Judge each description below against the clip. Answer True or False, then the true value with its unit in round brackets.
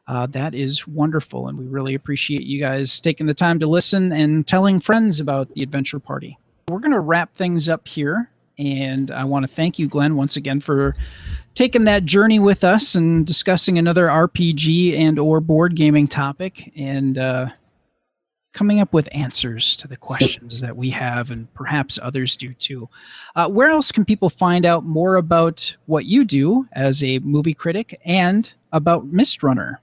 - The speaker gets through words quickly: False (180 wpm)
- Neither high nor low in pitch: True (155 Hz)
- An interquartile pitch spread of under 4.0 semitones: False (4.6 semitones)